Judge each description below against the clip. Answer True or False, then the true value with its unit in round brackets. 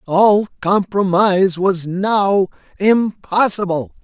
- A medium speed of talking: False (75 wpm)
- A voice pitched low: False (190 Hz)